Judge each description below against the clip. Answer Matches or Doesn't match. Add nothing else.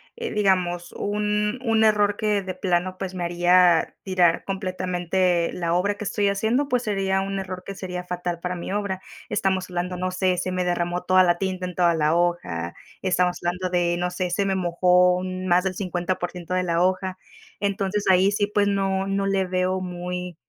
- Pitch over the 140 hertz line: Matches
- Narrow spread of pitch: Matches